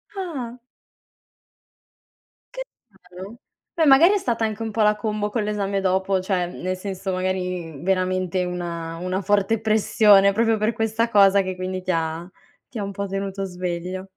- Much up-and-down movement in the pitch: No, average, 2.7 semitones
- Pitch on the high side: Yes, high, 195 Hz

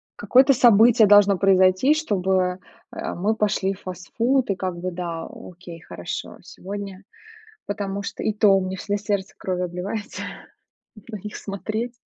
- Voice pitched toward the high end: Yes, high, 195 Hz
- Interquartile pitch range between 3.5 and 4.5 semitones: No, narrow, 2.5 semitones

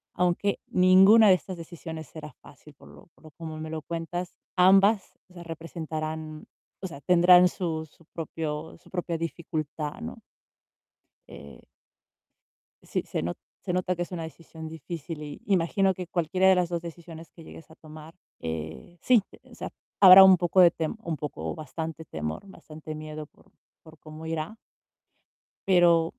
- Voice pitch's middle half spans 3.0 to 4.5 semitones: No, narrow, 2.5 semitones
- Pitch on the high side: No, medium, 165 Hz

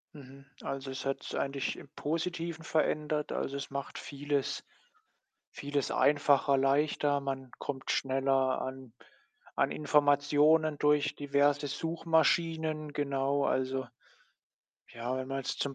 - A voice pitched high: No, medium, 140 Hz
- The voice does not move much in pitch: Yes, narrow, 1.7 semitones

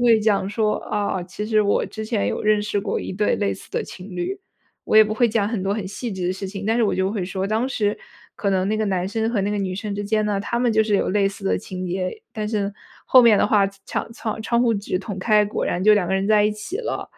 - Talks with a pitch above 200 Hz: Yes, high, 210 Hz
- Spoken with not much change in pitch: Yes, narrow, 2.0 semitones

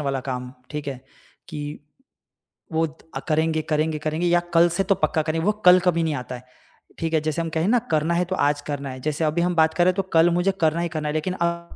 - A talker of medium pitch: Yes, medium, 160 Hz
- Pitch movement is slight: Yes, narrow, 2.2 semitones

